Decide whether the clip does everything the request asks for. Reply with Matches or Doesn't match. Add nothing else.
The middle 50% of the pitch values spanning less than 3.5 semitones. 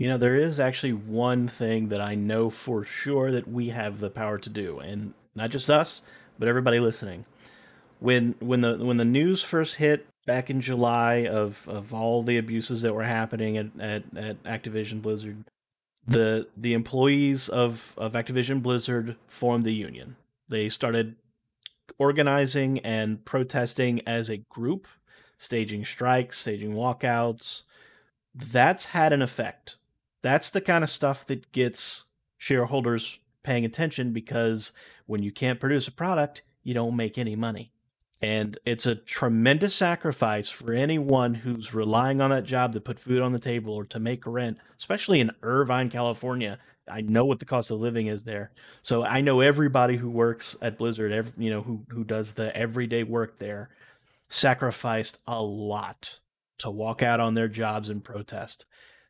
Matches